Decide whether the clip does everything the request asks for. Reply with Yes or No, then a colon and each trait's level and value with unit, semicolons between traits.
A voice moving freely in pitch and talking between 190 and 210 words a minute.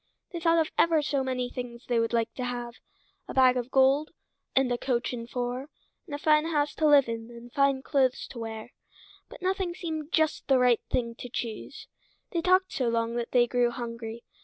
No: average, 4.0 semitones; fast, 205 wpm